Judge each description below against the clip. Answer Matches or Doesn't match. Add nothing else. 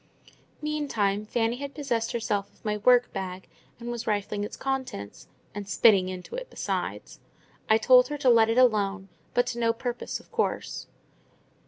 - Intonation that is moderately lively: Matches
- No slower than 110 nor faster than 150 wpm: Doesn't match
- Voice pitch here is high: Matches